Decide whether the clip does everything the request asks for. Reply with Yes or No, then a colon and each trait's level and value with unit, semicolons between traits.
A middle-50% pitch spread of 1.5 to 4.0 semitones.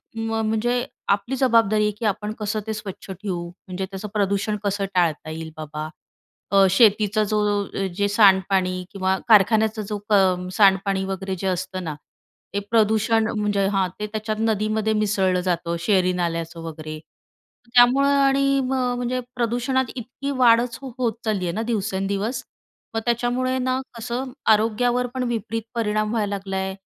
Yes: average, 3.4 semitones